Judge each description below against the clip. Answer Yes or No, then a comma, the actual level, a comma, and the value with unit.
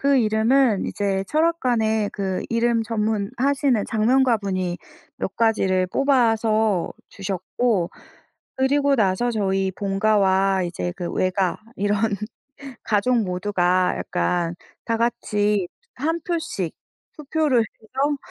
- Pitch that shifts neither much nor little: Yes, average, 4.4 semitones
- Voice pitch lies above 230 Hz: No, high, 215 Hz